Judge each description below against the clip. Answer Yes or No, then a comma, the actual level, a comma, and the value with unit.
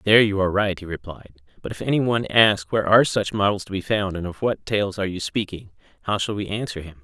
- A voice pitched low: Yes, low, 100 Hz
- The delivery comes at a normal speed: No, fast, 245 wpm